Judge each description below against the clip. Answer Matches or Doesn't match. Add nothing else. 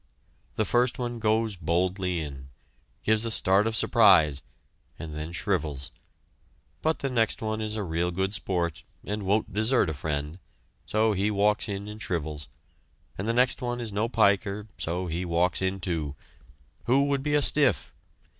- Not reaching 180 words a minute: Matches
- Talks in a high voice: Doesn't match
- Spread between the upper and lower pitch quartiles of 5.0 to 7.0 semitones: Doesn't match